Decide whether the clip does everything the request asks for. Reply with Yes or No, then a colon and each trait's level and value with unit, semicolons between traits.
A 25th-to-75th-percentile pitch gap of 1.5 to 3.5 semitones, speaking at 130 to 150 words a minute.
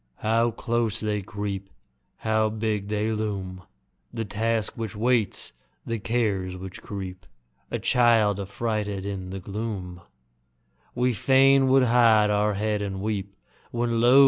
Yes: average, 2.7 semitones; slow, 135 wpm